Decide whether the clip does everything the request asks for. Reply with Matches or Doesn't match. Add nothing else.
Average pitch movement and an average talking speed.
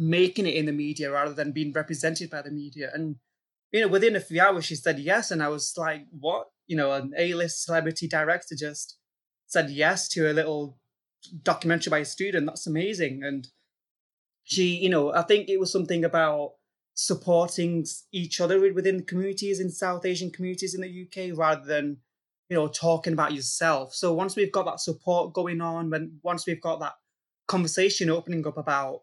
Matches